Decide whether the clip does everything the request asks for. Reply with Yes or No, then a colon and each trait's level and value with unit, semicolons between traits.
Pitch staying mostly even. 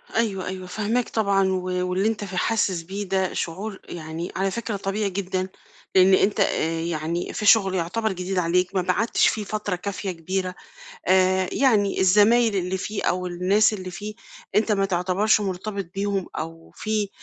Yes: narrow, 2.3 semitones